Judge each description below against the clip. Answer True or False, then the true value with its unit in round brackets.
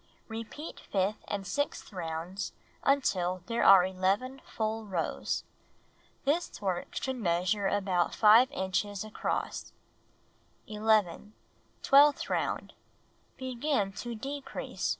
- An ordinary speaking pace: False (100 wpm)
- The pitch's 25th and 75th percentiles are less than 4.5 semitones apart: False (5.2 semitones)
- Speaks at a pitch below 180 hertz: False (210 Hz)